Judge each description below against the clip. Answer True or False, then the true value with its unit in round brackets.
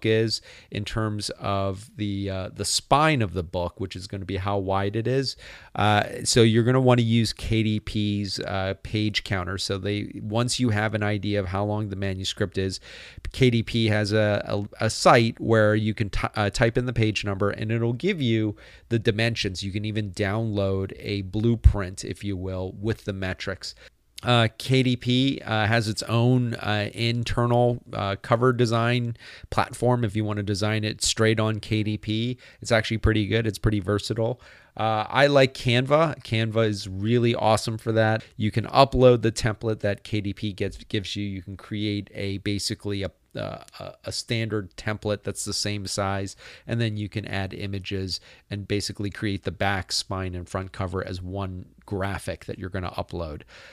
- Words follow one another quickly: False (185 wpm)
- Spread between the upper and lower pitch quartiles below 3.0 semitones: True (2.6 semitones)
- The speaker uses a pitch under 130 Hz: True (105 Hz)